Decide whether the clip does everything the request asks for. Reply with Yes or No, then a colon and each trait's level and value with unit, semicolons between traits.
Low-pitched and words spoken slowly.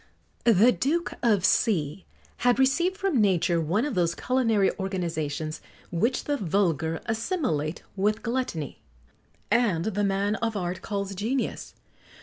No: high, 205 Hz; slow, 130 wpm